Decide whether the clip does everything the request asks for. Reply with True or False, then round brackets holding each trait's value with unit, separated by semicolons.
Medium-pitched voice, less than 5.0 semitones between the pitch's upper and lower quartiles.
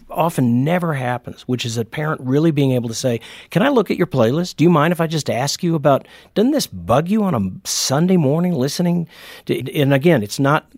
False (145 Hz; 5.4 semitones)